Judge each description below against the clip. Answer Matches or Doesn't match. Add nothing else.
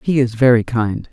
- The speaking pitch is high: Doesn't match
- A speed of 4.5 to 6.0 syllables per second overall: Matches